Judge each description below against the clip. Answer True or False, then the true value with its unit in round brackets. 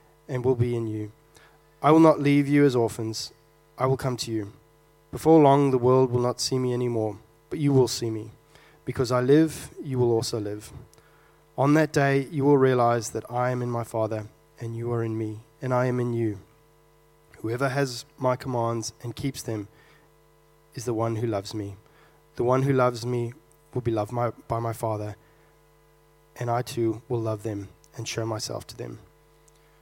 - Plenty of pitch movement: False (3.5 semitones)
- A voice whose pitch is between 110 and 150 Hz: True (120 Hz)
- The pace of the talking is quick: False (190 wpm)